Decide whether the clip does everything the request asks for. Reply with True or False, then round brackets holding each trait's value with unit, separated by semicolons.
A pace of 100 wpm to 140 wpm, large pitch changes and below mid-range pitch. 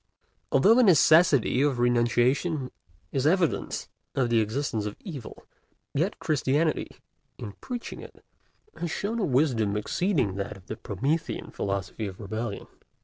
True (135 wpm; 6.7 semitones; 130 Hz)